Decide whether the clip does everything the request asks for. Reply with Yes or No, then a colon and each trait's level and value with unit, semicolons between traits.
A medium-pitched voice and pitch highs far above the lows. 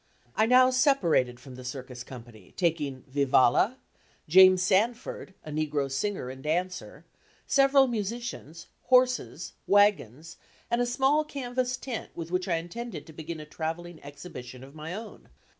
Yes: medium, 175 Hz; wide, 8.9 semitones